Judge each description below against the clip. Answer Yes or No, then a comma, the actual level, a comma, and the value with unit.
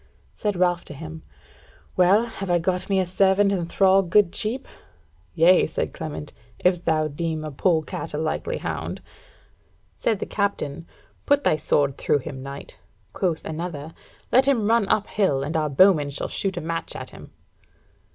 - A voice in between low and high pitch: Yes, medium, 175 Hz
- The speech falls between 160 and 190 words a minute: Yes, average, 170 wpm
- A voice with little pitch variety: No, average, 4.1 semitones